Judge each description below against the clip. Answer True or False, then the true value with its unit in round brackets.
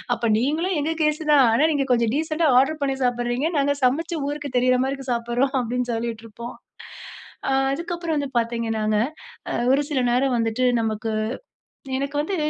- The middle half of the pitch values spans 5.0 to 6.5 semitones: False (3.9 semitones)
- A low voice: False (260 Hz)